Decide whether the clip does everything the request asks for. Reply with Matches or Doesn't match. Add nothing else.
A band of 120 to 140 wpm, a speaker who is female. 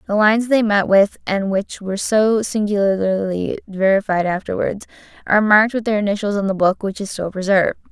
Doesn't match